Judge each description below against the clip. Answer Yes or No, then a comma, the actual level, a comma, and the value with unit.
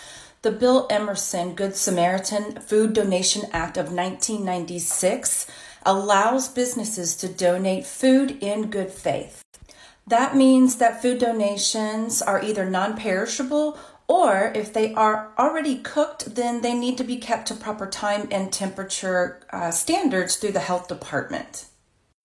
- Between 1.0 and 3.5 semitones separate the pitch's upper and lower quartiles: No, average, 4.2 semitones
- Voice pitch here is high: Yes, high, 210 Hz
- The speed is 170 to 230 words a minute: No, slow, 135 wpm